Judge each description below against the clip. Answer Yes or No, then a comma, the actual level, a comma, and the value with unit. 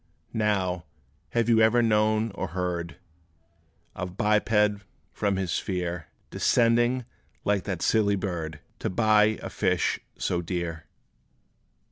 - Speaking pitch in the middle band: No, low, 100 Hz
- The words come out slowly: Yes, slow, 115 wpm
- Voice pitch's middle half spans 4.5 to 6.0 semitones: No, average, 3.4 semitones